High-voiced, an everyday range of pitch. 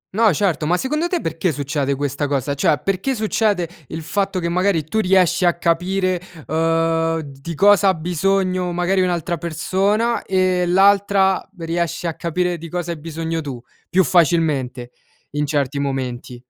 No: medium, 170 Hz; average, 3.7 semitones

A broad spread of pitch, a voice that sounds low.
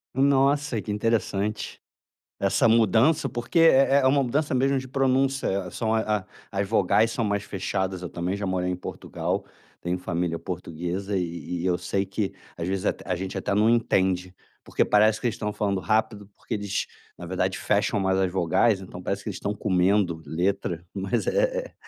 No: average, 3.8 semitones; low, 100 Hz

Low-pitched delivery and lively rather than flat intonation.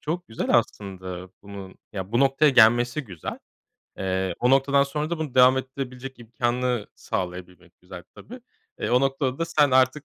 Yes: low, 125 Hz; wide, 5.9 semitones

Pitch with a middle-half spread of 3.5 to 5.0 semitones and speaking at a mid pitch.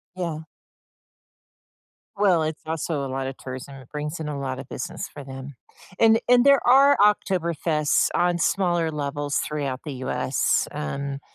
Yes: average, 4.3 semitones; medium, 150 Hz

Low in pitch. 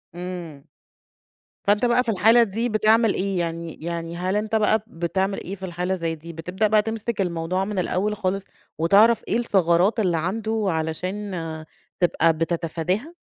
No: high, 190 Hz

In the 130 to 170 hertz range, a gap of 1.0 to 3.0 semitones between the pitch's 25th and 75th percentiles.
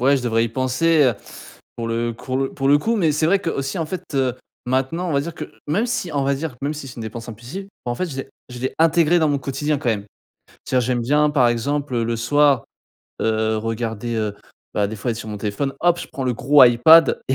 No: low, 135 Hz; average, 4.3 semitones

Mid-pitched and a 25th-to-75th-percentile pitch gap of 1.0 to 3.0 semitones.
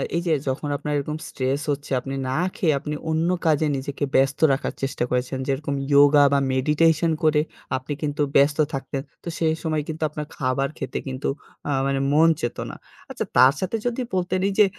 Yes: medium, 145 Hz; narrow, 2.6 semitones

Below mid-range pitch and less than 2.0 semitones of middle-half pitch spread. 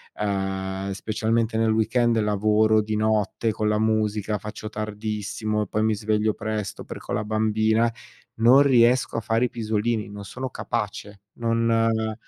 Yes: low, 110 Hz; narrow, 1.2 semitones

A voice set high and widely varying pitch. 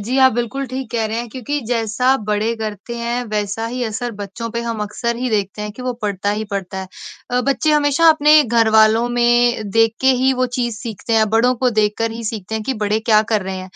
No: high, 230 Hz; narrow, 2.6 semitones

